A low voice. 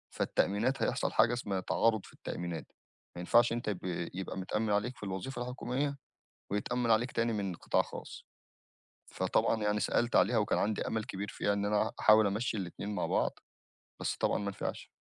Yes: low, 105 Hz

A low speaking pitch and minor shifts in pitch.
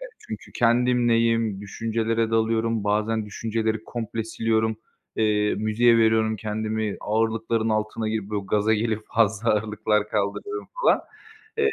Yes: low, 110 Hz; narrow, 1.2 semitones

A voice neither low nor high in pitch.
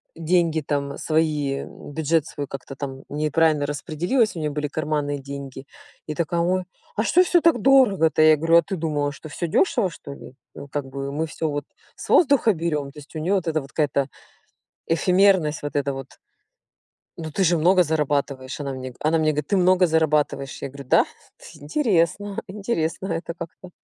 Yes: medium, 155 Hz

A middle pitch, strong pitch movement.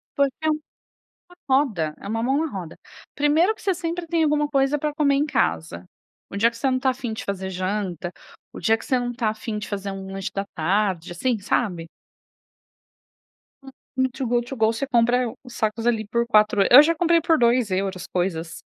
No: high, 235 Hz; wide, 6.0 semitones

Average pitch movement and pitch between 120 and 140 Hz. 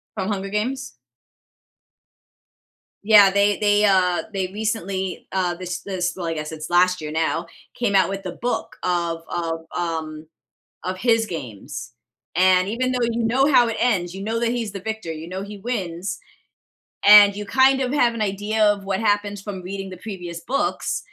No: average, 3.6 semitones; high, 195 Hz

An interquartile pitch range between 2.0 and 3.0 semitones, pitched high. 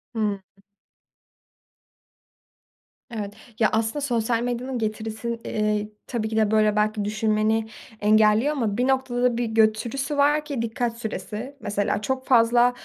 Yes: narrow, 2.4 semitones; high, 225 Hz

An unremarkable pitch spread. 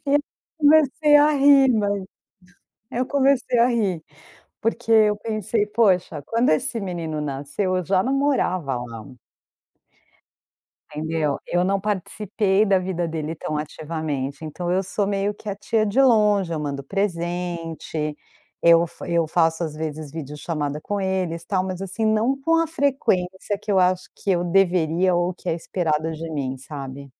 Yes: average, 4.9 semitones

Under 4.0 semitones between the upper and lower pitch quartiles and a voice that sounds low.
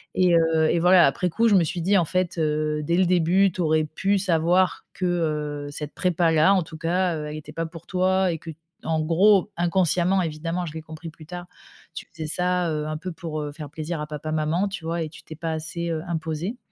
No: narrow, 2.5 semitones; medium, 165 Hz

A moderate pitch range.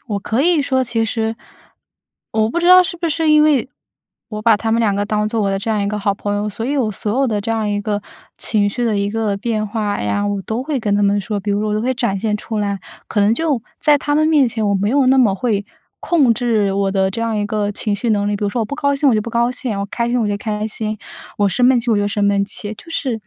Yes: average, 3.2 semitones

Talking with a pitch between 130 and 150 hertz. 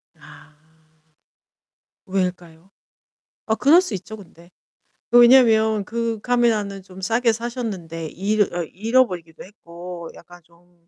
No: high, 195 Hz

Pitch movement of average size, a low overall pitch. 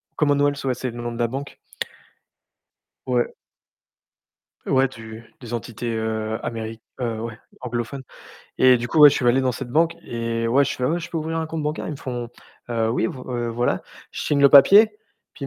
Yes: average, 3.5 semitones; low, 125 Hz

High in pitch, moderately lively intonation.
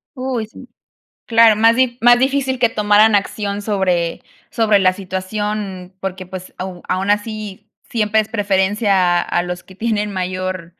Yes: high, 205 Hz; average, 3.0 semitones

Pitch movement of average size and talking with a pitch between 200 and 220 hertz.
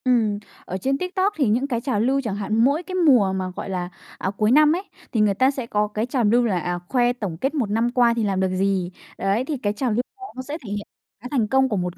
No: average, 4.7 semitones; high, 230 Hz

